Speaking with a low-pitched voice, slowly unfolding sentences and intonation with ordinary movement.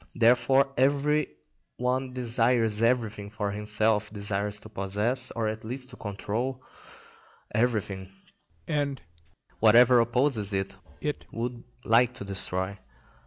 Yes: low, 115 Hz; slow, 115 wpm; average, 3.4 semitones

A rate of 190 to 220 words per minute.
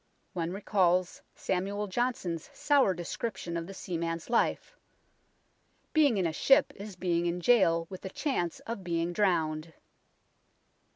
No: slow, 135 wpm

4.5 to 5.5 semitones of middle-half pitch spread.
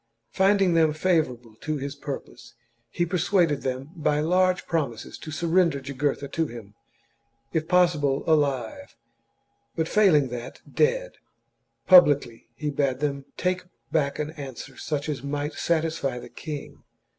No: average, 3.5 semitones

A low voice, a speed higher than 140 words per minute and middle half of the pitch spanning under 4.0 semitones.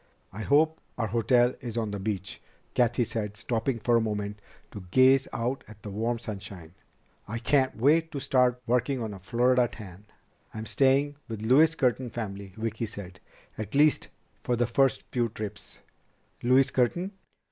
Yes: low, 115 Hz; average, 165 wpm; average, 3.6 semitones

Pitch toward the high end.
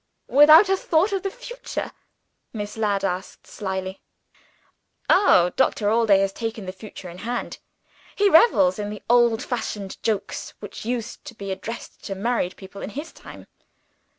Yes: high, 220 Hz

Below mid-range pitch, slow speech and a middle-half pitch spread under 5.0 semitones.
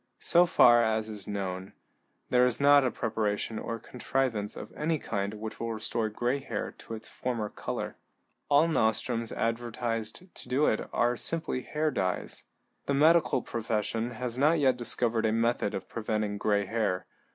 No: low, 115 Hz; average, 160 wpm; average, 2.8 semitones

